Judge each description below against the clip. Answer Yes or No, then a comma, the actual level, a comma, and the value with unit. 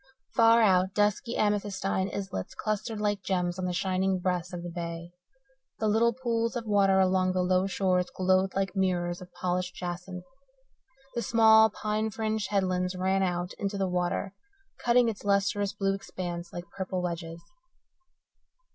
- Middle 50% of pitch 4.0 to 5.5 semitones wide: No, narrow, 2.5 semitones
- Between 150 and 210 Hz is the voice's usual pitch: Yes, high, 190 Hz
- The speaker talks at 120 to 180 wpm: Yes, average, 155 wpm